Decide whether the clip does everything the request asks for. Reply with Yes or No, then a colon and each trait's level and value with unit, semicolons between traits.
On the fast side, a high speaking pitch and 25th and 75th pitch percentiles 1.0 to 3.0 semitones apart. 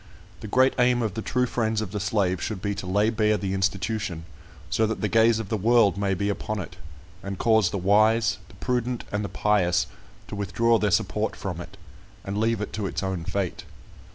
No: fast, 210 wpm; low, 105 Hz; narrow, 2.5 semitones